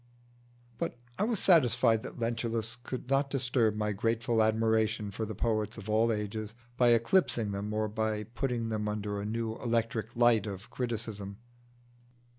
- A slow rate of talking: No, average, 155 wpm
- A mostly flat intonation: Yes, narrow, 1.8 semitones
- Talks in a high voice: No, low, 110 Hz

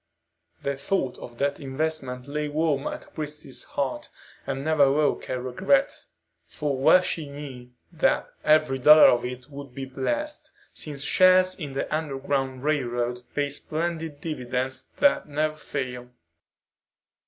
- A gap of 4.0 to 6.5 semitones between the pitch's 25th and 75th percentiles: No, average, 2.8 semitones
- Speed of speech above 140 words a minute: No, slow, 135 wpm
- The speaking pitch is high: No, medium, 140 Hz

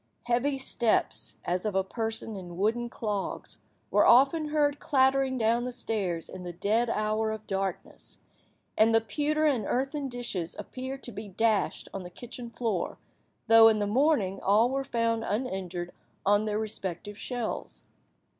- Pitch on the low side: No, high, 225 Hz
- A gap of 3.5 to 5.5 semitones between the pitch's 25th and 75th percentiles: Yes, average, 3.9 semitones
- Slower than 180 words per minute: Yes, average, 155 wpm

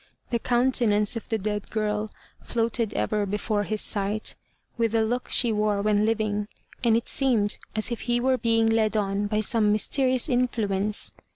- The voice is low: No, high, 220 Hz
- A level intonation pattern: Yes, narrow, 2.1 semitones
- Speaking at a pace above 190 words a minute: No, average, 170 wpm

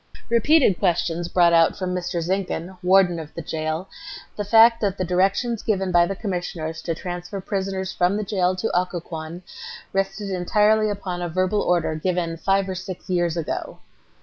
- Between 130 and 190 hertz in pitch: Yes, medium, 185 Hz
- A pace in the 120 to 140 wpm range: No, average, 170 wpm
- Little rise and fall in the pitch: Yes, narrow, 2.2 semitones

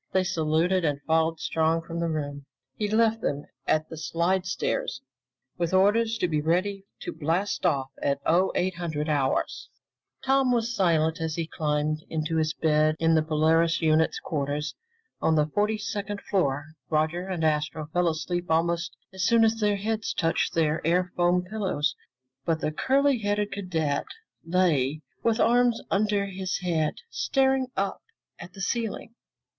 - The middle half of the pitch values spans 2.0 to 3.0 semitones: No, average, 4.3 semitones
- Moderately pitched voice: Yes, medium, 170 Hz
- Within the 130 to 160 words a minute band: Yes, average, 155 wpm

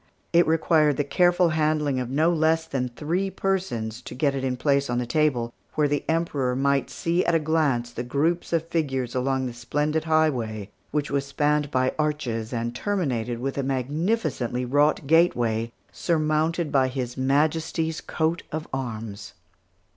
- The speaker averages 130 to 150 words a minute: No, average, 160 wpm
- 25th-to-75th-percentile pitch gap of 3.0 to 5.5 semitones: Yes, average, 4.1 semitones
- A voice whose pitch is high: No, medium, 145 Hz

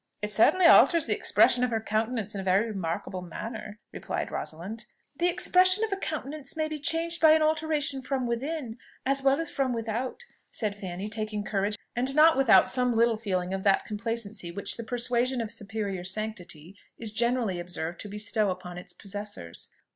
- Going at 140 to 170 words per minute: No, average, 180 wpm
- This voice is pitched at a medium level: No, high, 225 Hz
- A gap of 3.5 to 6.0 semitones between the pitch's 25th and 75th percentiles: Yes, average, 5.2 semitones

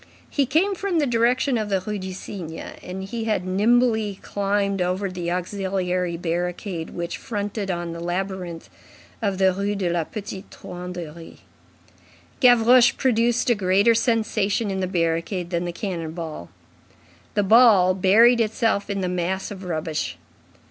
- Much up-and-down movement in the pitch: No, average, 3.7 semitones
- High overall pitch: Yes, high, 195 Hz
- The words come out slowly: No, average, 150 wpm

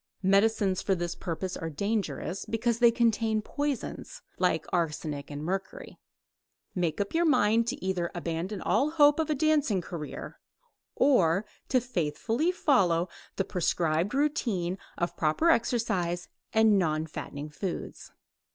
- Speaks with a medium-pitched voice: No, high, 195 Hz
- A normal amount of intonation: No, wide, 5.7 semitones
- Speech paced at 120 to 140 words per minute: Yes, slow, 135 wpm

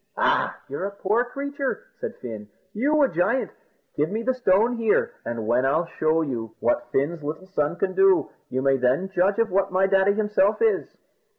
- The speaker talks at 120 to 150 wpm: No, average, 185 wpm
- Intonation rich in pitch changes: Yes, wide, 6.7 semitones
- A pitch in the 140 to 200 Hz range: Yes, high, 190 Hz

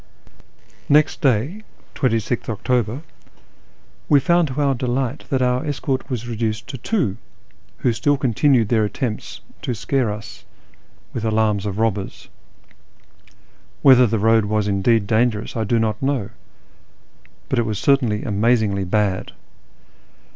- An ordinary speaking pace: No, slow, 130 wpm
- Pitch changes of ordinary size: Yes, average, 3.6 semitones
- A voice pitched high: No, low, 115 Hz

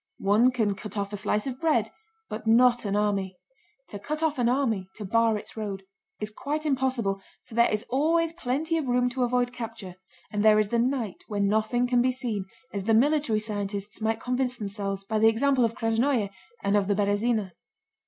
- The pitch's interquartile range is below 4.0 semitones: Yes, average, 3.4 semitones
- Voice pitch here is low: No, high, 225 Hz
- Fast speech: No, average, 195 wpm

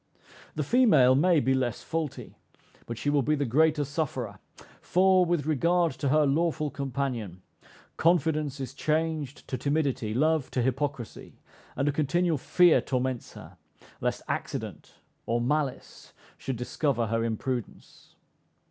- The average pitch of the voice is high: No, medium, 140 Hz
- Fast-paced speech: No, slow, 135 wpm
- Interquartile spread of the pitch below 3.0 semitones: No, average, 3.7 semitones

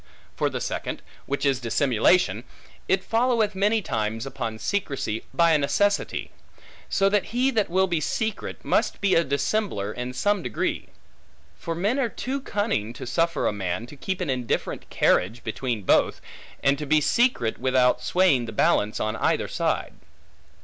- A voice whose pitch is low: No, medium, 150 Hz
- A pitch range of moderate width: No, wide, 9.0 semitones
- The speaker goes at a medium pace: Yes, average, 165 wpm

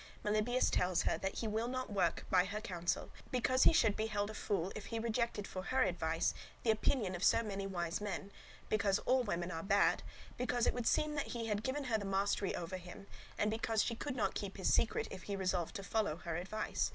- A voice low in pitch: No, high, 205 Hz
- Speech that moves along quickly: Yes, fast, 225 wpm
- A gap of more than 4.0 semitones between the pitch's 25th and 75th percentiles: No, average, 3.5 semitones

